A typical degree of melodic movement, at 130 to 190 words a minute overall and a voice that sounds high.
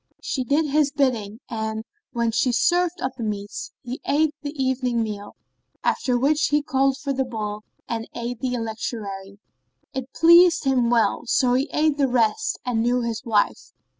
Yes: average, 3.7 semitones; average, 175 wpm; very high, 250 Hz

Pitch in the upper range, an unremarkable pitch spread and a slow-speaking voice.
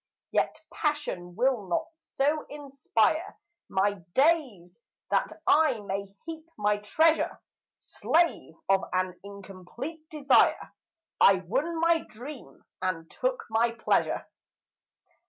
No: very high, 250 Hz; wide, 8.1 semitones; slow, 105 wpm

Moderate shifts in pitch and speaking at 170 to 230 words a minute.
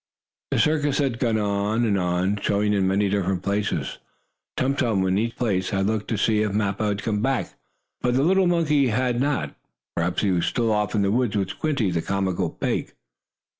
Yes: average, 3.9 semitones; average, 200 wpm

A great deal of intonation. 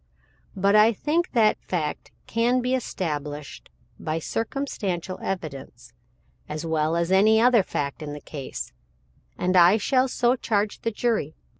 Yes: wide, 6.7 semitones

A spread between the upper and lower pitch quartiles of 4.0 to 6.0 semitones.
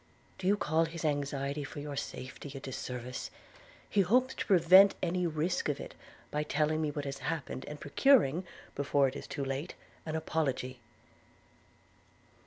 No: average, 3.5 semitones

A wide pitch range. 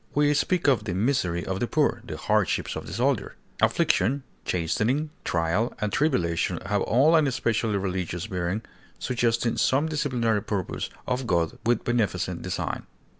Yes: wide, 6.2 semitones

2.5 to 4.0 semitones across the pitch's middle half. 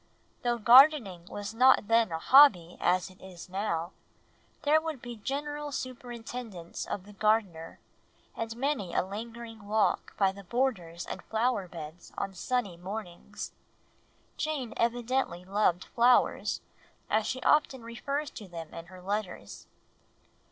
No: wide, 5.4 semitones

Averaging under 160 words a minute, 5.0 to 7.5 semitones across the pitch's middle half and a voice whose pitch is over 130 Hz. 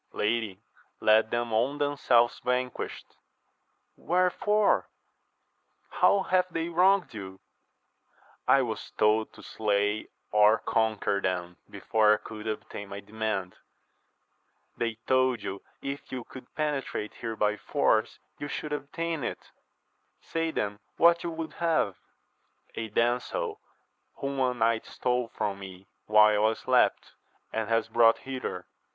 No: slow, 135 wpm; average, 5.3 semitones; low, 115 Hz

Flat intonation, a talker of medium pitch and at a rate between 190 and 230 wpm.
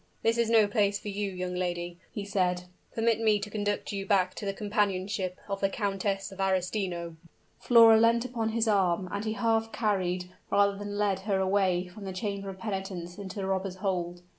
No: narrow, 2.2 semitones; high, 200 Hz; average, 195 wpm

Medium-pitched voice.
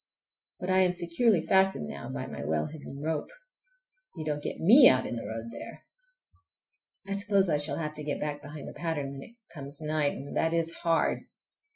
Yes: medium, 155 Hz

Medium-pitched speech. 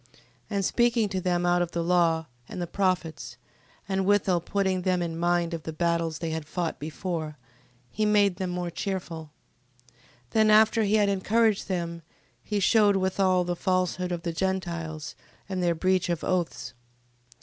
Yes: medium, 180 Hz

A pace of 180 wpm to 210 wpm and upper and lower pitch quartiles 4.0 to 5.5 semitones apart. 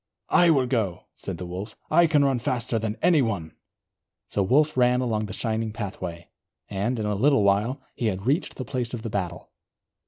Yes: average, 190 wpm; average, 4.4 semitones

